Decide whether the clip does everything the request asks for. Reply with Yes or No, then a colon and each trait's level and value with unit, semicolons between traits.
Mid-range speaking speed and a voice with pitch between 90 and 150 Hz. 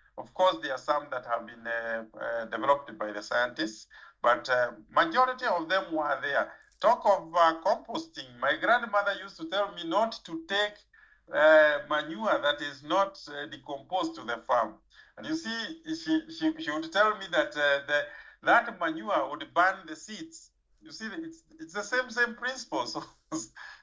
No: average, 180 wpm; high, 195 Hz